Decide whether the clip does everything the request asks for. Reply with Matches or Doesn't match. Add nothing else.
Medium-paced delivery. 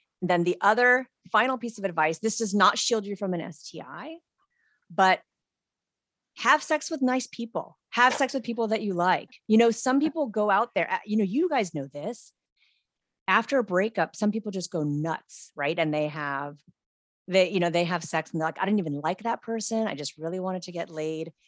Doesn't match